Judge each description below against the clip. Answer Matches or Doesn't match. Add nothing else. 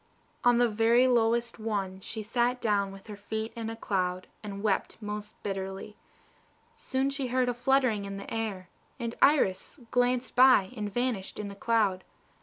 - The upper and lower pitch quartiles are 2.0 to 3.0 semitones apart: Doesn't match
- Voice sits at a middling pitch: Doesn't match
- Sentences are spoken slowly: Doesn't match